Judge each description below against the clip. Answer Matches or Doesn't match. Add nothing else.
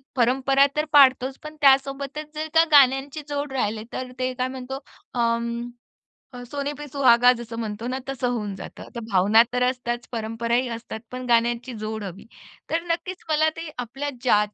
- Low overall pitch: Doesn't match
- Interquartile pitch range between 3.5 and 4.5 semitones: Doesn't match